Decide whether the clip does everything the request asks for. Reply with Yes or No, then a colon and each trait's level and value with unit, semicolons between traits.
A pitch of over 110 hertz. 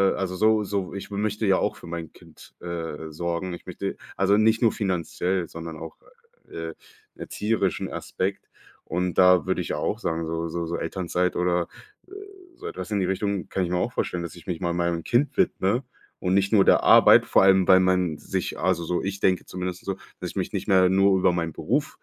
No: very low, 90 Hz